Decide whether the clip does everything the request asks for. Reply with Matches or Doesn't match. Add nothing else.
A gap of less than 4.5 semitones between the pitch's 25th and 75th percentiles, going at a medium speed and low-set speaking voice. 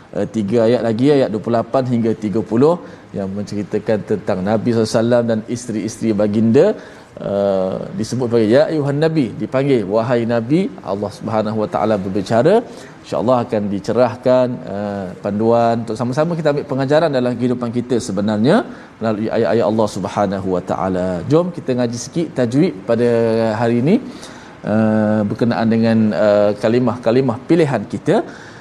Doesn't match